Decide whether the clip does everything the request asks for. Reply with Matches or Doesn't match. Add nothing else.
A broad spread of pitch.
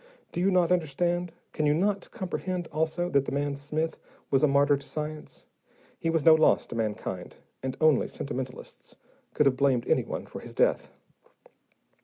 Doesn't match